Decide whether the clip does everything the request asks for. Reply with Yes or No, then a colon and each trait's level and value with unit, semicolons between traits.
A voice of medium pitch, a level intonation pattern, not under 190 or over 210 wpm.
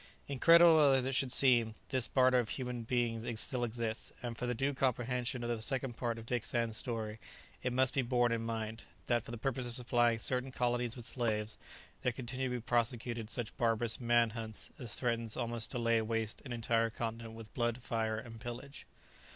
No: low, 120 Hz; narrow, 1.7 semitones; average, 200 wpm